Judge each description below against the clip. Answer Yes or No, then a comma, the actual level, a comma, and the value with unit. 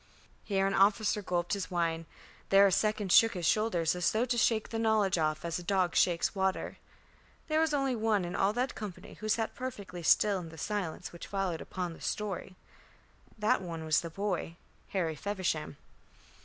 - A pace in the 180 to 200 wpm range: Yes, average, 185 wpm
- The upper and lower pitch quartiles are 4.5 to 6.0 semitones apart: No, average, 3.7 semitones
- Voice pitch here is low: No, high, 195 Hz